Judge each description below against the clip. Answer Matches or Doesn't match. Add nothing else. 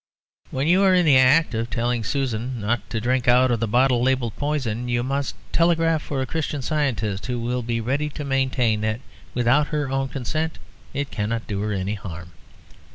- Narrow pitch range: Doesn't match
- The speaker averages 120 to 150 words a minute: Doesn't match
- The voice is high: Doesn't match